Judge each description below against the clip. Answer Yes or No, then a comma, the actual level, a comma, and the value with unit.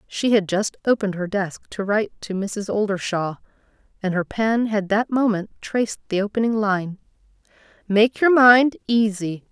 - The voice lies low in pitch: No, high, 210 Hz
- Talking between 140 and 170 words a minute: Yes, average, 160 wpm